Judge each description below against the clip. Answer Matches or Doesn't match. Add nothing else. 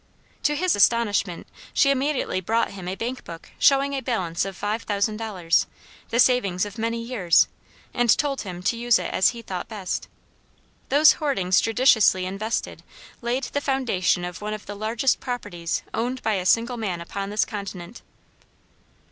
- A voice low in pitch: Doesn't match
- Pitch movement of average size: Matches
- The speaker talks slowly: Doesn't match